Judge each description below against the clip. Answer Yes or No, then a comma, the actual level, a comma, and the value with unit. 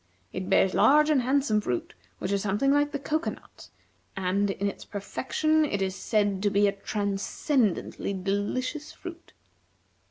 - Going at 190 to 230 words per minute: No, average, 140 wpm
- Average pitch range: No, wide, 6.5 semitones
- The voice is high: Yes, high, 205 Hz